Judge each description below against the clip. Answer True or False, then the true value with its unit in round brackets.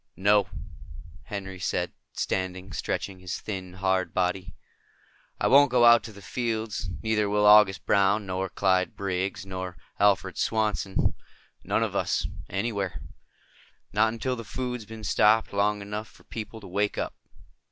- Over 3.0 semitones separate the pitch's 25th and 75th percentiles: False (2.5 semitones)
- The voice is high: False (100 Hz)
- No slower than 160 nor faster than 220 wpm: False (145 wpm)